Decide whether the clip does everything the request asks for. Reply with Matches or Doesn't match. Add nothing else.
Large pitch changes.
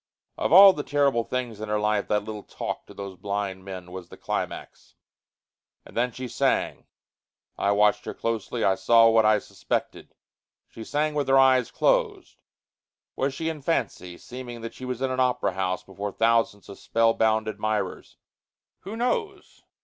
Doesn't match